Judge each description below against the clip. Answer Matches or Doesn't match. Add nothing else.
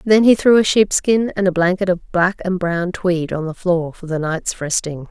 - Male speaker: Doesn't match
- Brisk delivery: Matches